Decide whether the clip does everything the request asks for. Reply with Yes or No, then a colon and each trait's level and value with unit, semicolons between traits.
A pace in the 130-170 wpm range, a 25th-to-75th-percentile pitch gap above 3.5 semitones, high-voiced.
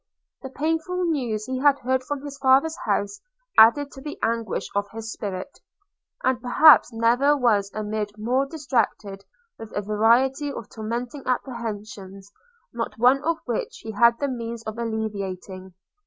Yes: average, 155 wpm; average, 4.3 semitones; high, 235 Hz